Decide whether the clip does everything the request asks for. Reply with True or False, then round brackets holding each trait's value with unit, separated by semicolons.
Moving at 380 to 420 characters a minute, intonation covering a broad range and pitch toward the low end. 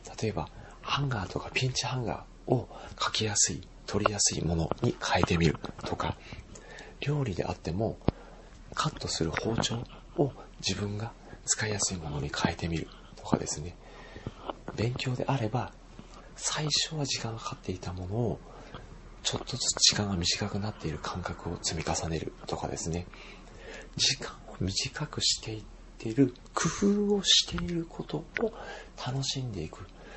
False (300 characters per minute; 6.4 semitones; 105 Hz)